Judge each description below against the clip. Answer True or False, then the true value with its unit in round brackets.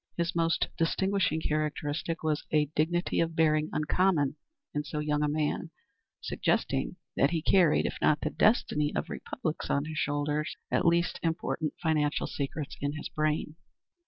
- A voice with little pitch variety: True (1.8 semitones)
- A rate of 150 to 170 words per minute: True (155 wpm)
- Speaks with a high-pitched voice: False (155 Hz)